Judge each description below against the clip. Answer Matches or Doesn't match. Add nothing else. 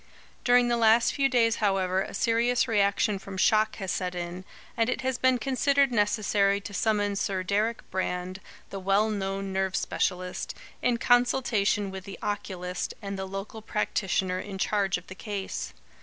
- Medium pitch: Doesn't match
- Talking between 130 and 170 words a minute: Matches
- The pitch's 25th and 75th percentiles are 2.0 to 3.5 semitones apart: Matches